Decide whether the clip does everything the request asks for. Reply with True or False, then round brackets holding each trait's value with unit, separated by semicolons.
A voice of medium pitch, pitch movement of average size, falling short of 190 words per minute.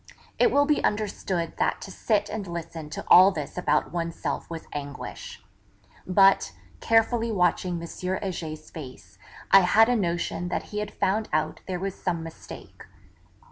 True (180 Hz; 4.0 semitones; 155 wpm)